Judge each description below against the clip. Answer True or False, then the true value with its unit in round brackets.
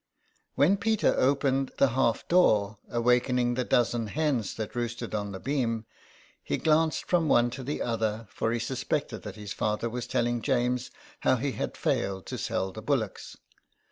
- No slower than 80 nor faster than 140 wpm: False (170 wpm)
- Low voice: True (120 Hz)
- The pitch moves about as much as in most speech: True (3.5 semitones)